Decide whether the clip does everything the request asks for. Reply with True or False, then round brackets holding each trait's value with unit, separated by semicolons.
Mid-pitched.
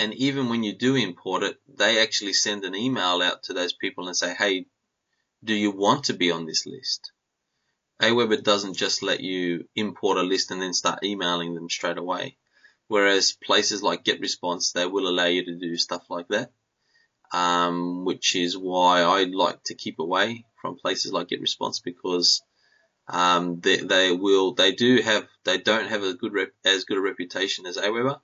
False (95 Hz)